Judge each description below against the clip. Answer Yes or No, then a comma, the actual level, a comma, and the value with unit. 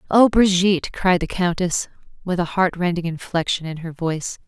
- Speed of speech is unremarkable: Yes, average, 175 wpm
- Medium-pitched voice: Yes, medium, 175 Hz